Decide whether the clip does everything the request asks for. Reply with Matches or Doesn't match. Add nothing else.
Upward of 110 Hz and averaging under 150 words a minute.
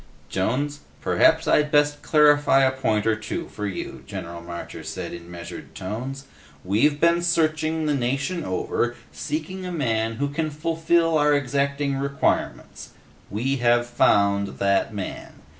Matches